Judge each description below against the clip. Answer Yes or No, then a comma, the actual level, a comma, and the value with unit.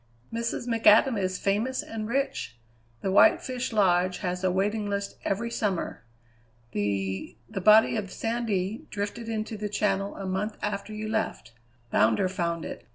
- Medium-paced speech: Yes, average, 155 wpm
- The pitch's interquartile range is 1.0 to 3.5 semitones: Yes, average, 3.0 semitones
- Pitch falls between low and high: No, high, 205 Hz